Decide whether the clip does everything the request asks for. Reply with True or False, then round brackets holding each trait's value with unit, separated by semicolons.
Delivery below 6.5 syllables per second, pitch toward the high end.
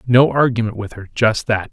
False (5.3 syllables/s; 115 Hz)